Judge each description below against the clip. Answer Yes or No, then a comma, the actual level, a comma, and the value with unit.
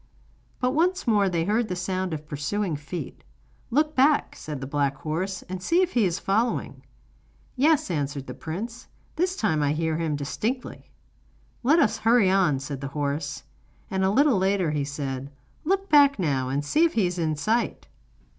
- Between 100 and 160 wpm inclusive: No, average, 180 wpm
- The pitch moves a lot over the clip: Yes, wide, 8.5 semitones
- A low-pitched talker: No, medium, 185 Hz